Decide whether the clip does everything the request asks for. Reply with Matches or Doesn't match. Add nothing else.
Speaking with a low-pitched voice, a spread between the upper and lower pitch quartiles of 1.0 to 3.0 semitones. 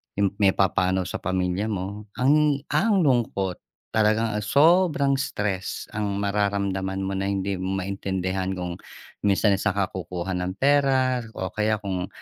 Matches